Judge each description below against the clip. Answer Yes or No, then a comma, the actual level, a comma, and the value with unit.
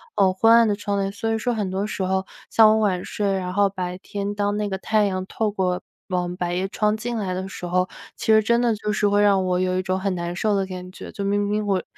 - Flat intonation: Yes, narrow, 2.2 semitones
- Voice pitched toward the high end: Yes, high, 200 Hz